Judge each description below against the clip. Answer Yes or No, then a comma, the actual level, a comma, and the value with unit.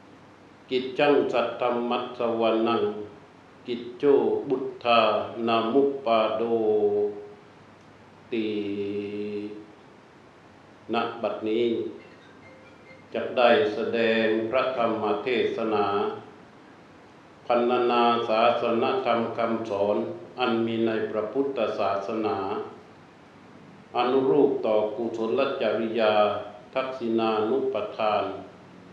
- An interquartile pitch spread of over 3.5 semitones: No, narrow, 2.4 semitones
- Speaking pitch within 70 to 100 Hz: No, low, 115 Hz